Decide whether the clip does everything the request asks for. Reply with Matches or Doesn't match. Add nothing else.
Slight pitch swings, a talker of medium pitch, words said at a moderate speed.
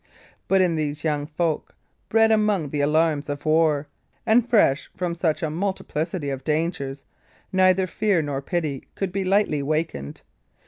Doesn't match